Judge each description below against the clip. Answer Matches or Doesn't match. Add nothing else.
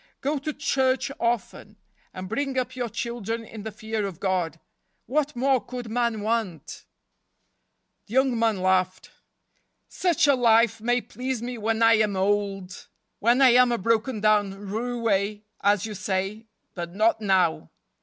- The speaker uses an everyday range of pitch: Matches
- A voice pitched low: Doesn't match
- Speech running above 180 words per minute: Doesn't match